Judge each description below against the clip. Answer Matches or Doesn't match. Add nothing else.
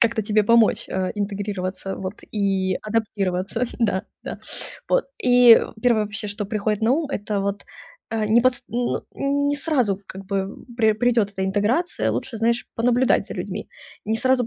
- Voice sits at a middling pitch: Doesn't match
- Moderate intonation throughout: Matches